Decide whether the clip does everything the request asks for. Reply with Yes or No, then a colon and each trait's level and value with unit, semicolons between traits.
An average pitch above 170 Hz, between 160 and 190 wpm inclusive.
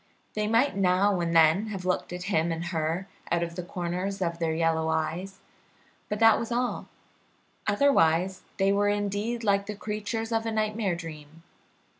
Yes: high, 190 Hz; average, 170 wpm